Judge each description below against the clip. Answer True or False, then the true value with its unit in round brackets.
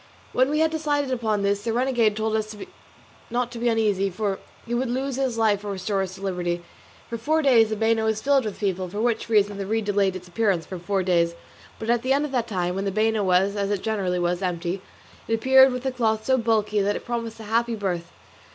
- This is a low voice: False (220 Hz)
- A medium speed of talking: False (240 wpm)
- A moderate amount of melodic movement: True (3.5 semitones)